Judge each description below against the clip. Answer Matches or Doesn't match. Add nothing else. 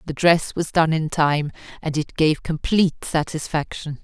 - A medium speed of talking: Matches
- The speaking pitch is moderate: Matches